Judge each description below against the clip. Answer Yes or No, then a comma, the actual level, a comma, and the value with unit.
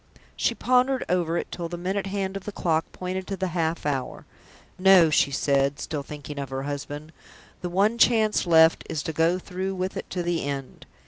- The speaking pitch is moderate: Yes, medium, 175 Hz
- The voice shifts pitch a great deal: No, average, 4.3 semitones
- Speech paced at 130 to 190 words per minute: No, average, 200 wpm